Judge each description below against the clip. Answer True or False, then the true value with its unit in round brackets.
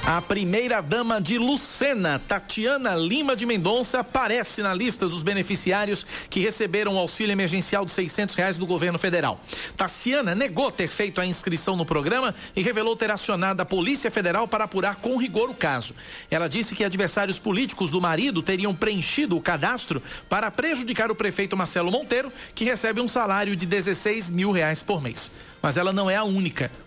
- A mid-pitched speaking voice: False (200 Hz)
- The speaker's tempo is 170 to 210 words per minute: True (180 wpm)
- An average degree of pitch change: True (3.9 semitones)